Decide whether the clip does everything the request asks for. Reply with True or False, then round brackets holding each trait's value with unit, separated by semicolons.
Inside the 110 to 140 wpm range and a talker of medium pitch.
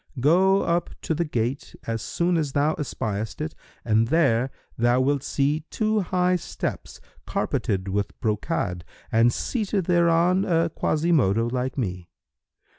True (135 wpm; 145 Hz)